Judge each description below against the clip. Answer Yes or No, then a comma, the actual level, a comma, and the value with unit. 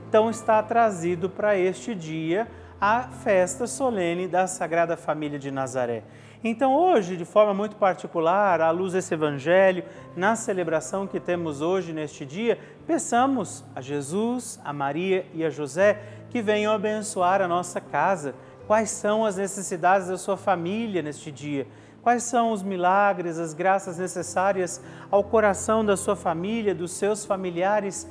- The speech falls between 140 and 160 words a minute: Yes, average, 145 wpm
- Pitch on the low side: No, medium, 185 Hz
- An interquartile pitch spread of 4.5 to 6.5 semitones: No, average, 3.9 semitones